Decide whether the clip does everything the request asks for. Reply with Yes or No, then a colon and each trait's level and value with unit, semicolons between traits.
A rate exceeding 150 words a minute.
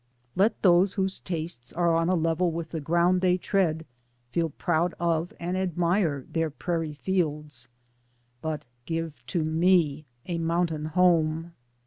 No: average, 145 wpm